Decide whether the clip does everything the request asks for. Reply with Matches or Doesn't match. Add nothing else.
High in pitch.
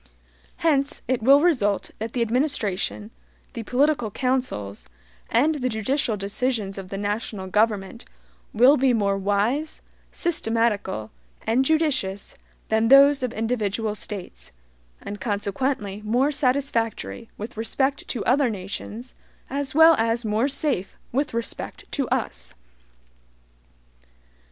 Matches